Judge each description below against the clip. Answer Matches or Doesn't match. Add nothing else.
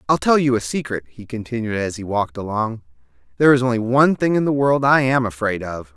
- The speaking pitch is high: Doesn't match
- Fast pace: Matches